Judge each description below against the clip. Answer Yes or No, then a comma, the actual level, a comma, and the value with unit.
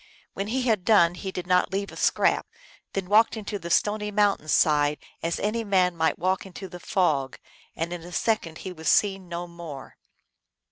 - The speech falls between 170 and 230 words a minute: Yes, average, 190 wpm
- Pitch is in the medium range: Yes, medium, 180 Hz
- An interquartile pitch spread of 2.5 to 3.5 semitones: Yes, average, 3.2 semitones